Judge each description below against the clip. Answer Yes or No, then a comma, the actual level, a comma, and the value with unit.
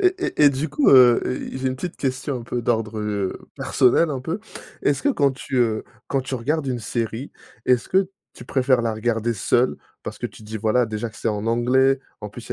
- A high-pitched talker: No, low, 125 Hz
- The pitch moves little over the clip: No, average, 3.1 semitones